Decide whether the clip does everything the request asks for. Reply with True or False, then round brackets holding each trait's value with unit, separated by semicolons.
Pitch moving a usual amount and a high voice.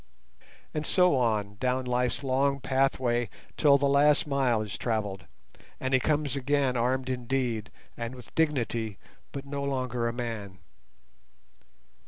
False (3.0 semitones; 130 Hz)